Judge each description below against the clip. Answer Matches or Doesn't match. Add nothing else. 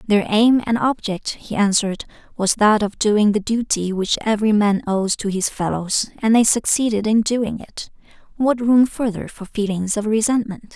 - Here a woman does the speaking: Matches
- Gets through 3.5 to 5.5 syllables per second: Matches